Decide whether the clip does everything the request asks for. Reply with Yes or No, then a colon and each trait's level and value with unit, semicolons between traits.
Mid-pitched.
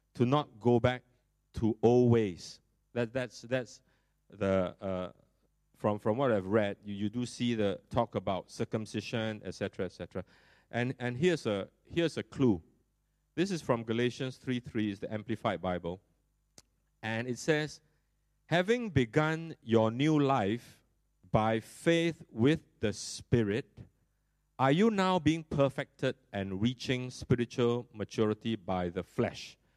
No: low, 120 Hz